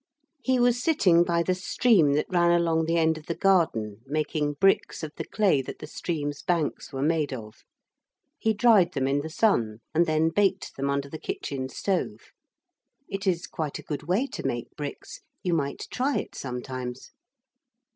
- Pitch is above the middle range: No, medium, 160 Hz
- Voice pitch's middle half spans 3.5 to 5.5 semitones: Yes, average, 4.7 semitones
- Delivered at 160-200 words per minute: Yes, average, 180 wpm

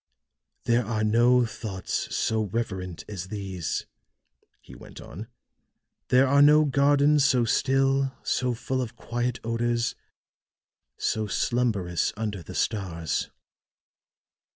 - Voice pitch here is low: Yes, low, 115 Hz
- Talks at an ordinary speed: No, slow, 110 wpm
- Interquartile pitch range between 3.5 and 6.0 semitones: Yes, average, 4.1 semitones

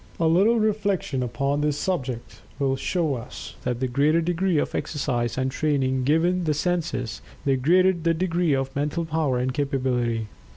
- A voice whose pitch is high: No, medium, 145 Hz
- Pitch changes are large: No, average, 4.6 semitones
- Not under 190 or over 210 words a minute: No, average, 165 wpm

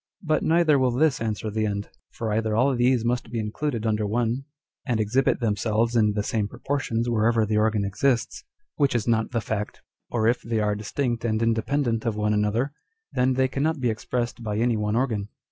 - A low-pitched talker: Yes, low, 115 Hz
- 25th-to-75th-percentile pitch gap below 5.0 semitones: Yes, average, 2.8 semitones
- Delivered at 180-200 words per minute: Yes, average, 195 wpm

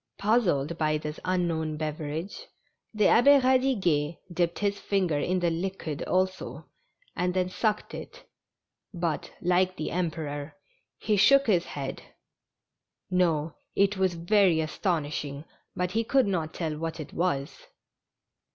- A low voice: No, medium, 175 Hz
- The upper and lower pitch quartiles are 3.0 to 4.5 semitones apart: Yes, average, 3.9 semitones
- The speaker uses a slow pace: Yes, slow, 130 wpm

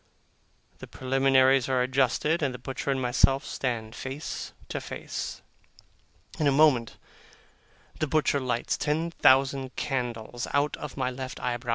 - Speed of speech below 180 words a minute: Yes, average, 140 wpm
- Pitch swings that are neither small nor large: No, narrow, 1.9 semitones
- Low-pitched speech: Yes, low, 130 Hz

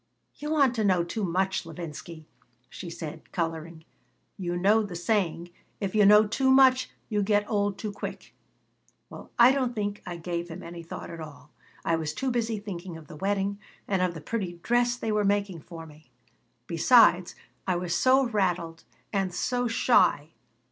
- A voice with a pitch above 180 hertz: Yes, high, 190 Hz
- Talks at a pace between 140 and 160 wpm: No, average, 175 wpm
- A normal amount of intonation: Yes, average, 4.3 semitones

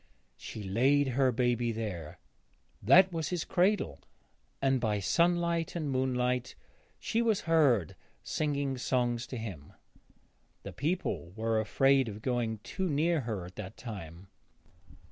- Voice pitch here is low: Yes, low, 125 Hz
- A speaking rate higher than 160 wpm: No, slow, 135 wpm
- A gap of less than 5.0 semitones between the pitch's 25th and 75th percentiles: No, wide, 5.5 semitones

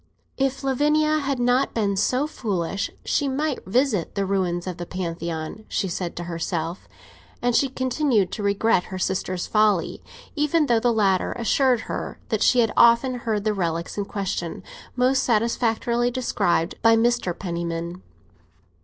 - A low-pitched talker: No, high, 220 Hz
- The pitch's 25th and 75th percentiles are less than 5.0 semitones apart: No, wide, 5.5 semitones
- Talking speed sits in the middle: Yes, average, 155 wpm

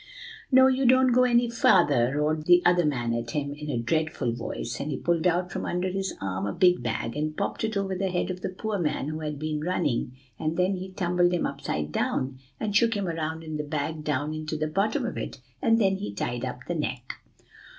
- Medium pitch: Yes, medium, 160 Hz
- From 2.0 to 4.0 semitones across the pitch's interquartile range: No, average, 4.7 semitones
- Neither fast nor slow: No, fast, 230 wpm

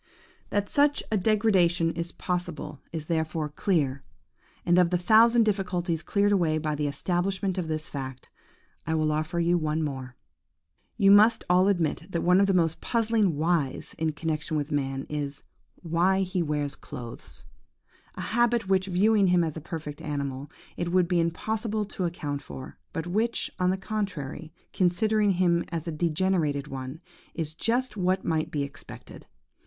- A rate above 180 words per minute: No, average, 165 wpm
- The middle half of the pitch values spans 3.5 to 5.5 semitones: Yes, average, 4.0 semitones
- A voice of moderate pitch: Yes, medium, 170 Hz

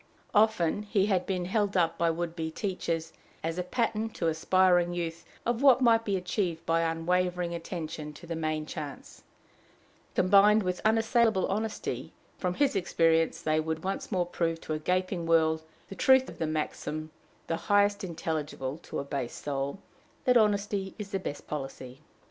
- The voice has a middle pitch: Yes, medium, 175 Hz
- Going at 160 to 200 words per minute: Yes, average, 165 wpm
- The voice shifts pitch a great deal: No, average, 3.9 semitones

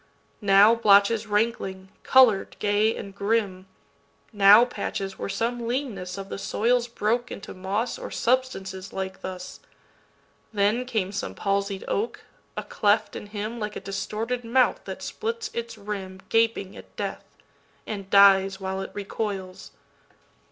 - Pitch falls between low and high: No, high, 205 Hz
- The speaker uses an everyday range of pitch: Yes, average, 3.1 semitones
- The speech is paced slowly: Yes, slow, 125 wpm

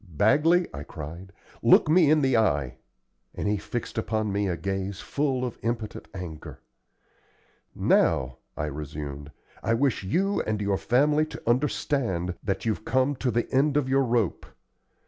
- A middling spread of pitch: No, wide, 6.6 semitones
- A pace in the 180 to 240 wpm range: No, average, 155 wpm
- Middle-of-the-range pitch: No, low, 110 Hz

